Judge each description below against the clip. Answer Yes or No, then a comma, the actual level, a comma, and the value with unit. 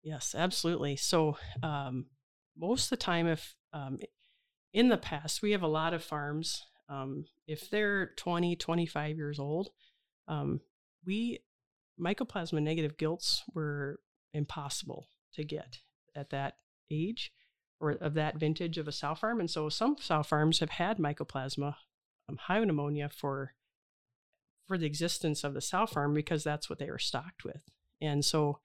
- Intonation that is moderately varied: Yes, average, 3.1 semitones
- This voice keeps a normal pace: Yes, average, 155 wpm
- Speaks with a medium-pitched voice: Yes, medium, 155 Hz